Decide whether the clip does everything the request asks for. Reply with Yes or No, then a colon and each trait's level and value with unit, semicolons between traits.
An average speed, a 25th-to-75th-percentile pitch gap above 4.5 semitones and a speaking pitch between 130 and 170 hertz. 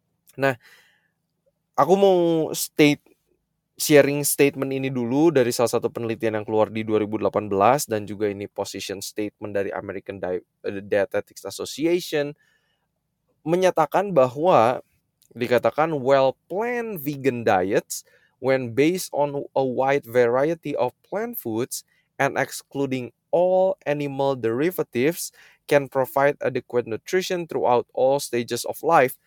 Yes: average, 115 wpm; average, 5.1 semitones; medium, 140 Hz